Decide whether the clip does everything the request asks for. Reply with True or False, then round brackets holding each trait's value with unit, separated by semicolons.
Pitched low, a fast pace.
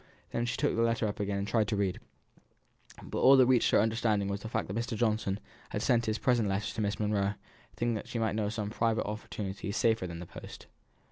True (110 Hz; 235 wpm)